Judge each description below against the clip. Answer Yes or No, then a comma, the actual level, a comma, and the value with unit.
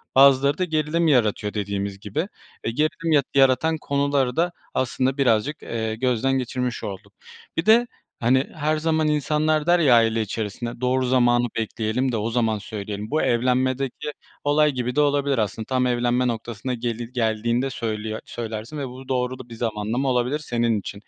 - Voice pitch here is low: Yes, low, 125 Hz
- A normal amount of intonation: Yes, average, 3.8 semitones